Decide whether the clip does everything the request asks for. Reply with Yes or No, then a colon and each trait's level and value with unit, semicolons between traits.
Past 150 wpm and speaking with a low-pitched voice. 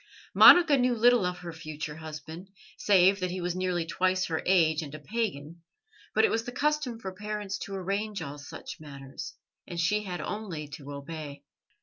No: average, 185 wpm; medium, 180 Hz